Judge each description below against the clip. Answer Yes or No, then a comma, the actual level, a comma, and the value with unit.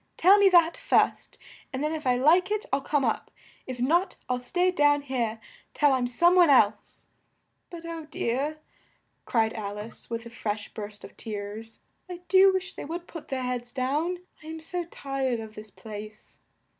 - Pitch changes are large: Yes, wide, 6.7 semitones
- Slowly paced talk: No, average, 185 wpm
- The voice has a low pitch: No, very high, 270 Hz